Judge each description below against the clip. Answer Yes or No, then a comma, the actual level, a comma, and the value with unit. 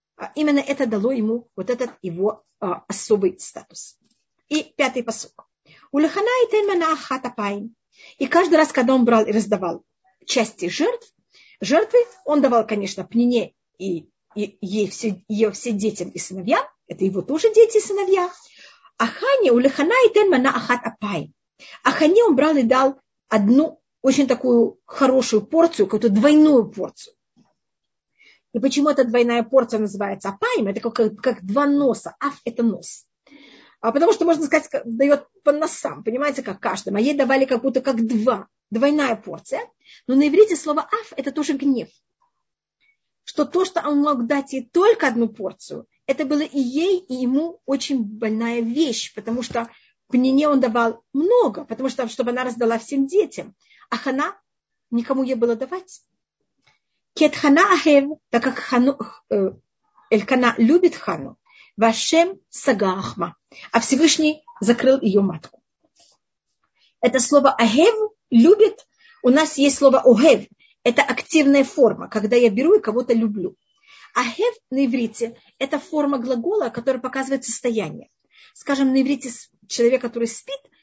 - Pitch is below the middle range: No, very high, 265 Hz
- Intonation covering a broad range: No, average, 4.7 semitones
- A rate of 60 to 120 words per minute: No, average, 145 wpm